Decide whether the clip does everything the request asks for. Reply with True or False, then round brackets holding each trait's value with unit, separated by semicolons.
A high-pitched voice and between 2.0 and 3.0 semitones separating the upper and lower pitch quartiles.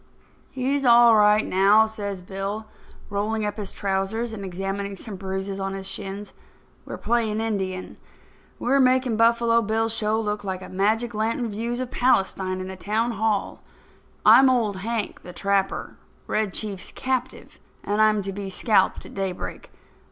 True (210 Hz; 2.7 semitones)